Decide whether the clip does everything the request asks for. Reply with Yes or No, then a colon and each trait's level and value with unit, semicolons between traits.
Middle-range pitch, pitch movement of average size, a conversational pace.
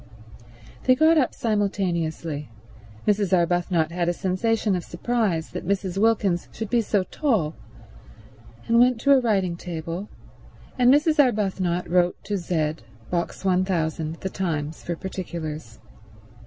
No: medium, 180 Hz; average, 4.5 semitones; slow, 125 wpm